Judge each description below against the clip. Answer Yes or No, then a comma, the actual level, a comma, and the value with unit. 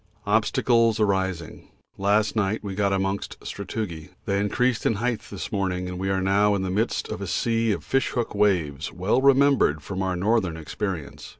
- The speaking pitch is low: Yes, low, 100 Hz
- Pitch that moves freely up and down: No, average, 2.9 semitones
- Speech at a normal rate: Yes, average, 180 wpm